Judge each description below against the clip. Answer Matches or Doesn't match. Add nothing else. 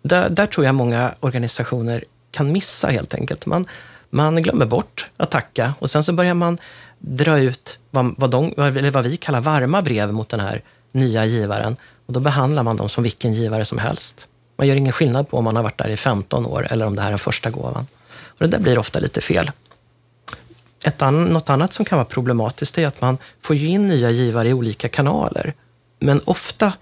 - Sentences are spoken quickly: Matches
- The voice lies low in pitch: Matches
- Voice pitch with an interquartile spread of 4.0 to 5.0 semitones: Matches